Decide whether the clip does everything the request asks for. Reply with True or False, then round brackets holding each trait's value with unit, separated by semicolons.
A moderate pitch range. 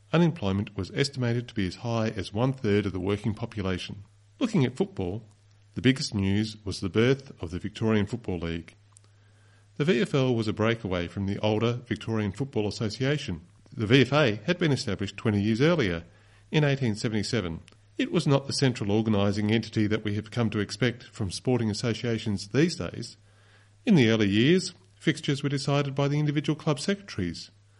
True (4.2 semitones)